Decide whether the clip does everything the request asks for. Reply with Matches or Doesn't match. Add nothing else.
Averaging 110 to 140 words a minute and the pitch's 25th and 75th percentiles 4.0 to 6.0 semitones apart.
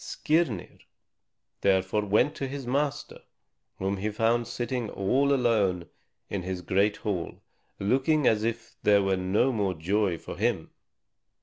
Matches